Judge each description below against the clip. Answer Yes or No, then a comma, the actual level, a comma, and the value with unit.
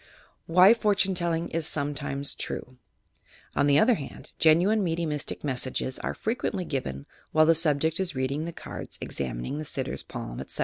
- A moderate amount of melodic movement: Yes, average, 4.1 semitones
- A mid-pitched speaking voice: Yes, medium, 155 Hz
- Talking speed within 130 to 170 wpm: Yes, average, 160 wpm